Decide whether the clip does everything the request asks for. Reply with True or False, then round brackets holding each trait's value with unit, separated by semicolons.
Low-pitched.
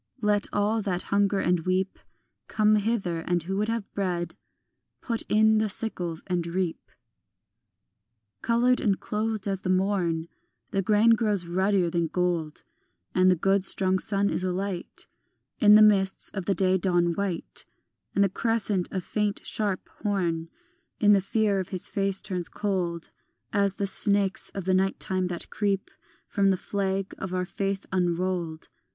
False (195 Hz)